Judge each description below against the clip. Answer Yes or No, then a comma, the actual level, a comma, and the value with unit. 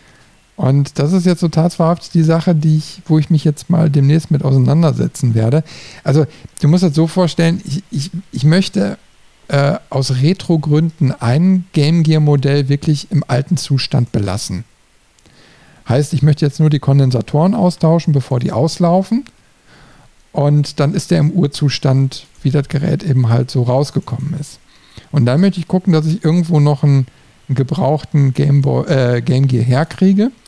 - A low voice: No, medium, 150 Hz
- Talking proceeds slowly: No, average, 160 wpm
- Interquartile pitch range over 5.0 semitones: No, average, 3.5 semitones